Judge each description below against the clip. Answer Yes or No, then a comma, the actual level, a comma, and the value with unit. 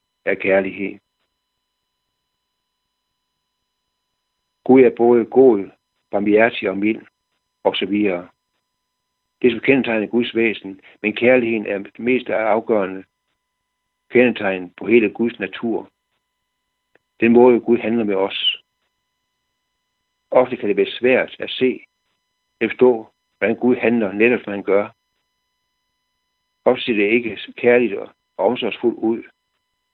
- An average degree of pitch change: Yes, average, 3.8 semitones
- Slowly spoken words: Yes, slow, 115 wpm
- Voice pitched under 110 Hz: No, low, 115 Hz